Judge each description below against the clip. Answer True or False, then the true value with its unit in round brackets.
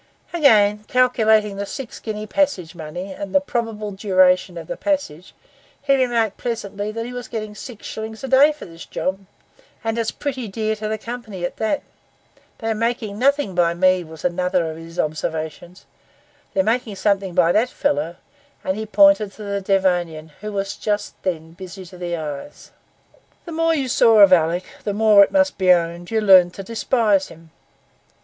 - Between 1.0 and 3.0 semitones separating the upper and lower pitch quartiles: False (4.2 semitones)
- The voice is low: False (205 Hz)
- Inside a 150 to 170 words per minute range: False (180 wpm)